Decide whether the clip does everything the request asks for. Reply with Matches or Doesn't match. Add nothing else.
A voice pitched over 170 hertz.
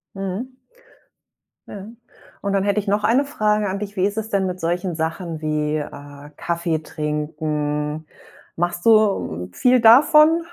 Matches